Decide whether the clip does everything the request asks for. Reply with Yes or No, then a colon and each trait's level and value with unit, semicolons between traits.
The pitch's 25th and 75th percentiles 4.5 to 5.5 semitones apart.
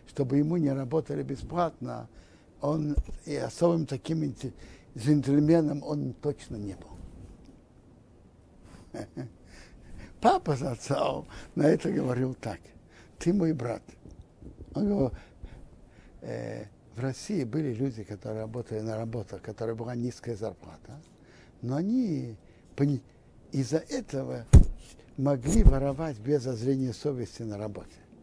Yes: average, 5.0 semitones